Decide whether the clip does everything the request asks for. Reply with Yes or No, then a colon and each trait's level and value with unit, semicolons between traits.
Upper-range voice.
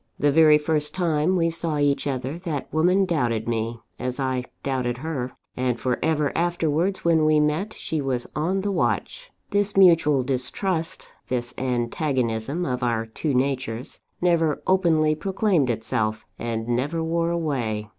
No: medium, 150 Hz